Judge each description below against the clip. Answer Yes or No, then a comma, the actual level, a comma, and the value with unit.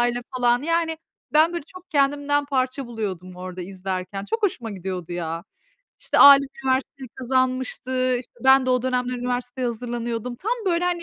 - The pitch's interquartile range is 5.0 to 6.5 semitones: No, average, 3.7 semitones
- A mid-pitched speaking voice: No, very high, 250 Hz